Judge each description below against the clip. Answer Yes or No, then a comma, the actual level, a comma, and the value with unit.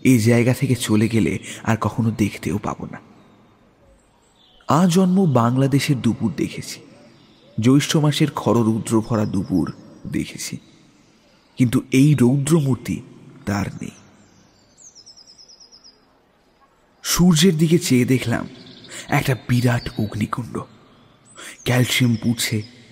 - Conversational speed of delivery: Yes, average, 90 wpm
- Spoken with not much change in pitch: No, average, 3.7 semitones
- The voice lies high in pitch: No, low, 120 Hz